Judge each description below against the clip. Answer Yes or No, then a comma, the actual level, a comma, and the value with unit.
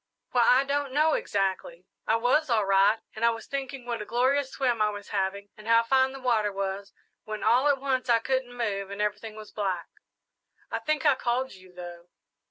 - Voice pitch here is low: No, high, 230 Hz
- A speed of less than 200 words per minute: No, fast, 205 wpm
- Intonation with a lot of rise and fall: No, average, 4.4 semitones